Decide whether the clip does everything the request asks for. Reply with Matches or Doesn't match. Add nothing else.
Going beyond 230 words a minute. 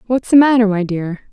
Doesn't match